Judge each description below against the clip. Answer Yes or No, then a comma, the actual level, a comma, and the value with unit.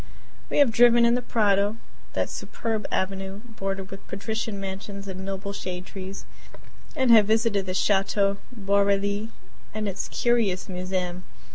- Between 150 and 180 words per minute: No, average, 140 wpm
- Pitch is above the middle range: Yes, high, 200 Hz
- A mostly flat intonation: Yes, narrow, 2.3 semitones